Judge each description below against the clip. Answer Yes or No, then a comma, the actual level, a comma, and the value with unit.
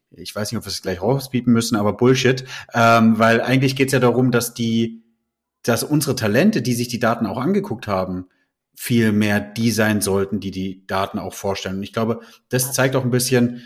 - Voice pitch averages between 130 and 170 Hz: No, low, 115 Hz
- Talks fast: Yes, fast, 210 wpm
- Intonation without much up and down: No, average, 3.1 semitones